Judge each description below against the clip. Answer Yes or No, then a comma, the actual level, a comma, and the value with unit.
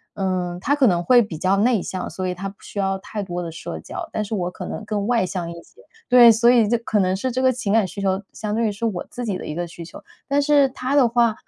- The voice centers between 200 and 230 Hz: Yes, high, 205 Hz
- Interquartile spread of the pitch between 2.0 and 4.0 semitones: No, average, 4.5 semitones